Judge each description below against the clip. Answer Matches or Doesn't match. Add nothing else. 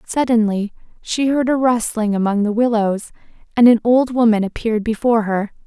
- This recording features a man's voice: Doesn't match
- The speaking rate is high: Doesn't match